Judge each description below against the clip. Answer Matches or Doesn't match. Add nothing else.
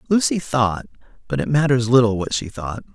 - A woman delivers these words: Doesn't match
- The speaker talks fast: Doesn't match